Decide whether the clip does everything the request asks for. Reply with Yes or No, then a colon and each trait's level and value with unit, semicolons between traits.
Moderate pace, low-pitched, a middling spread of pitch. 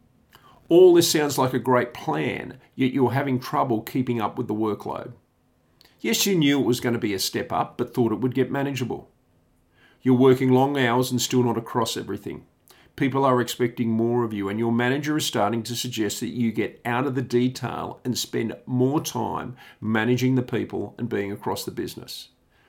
No: average, 195 wpm; low, 125 Hz; narrow, 1.9 semitones